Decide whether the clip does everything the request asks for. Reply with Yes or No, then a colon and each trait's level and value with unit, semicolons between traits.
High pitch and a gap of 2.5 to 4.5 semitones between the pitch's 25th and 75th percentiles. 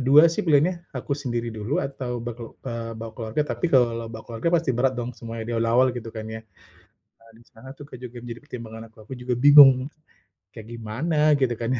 No: low, 120 Hz; average, 2.9 semitones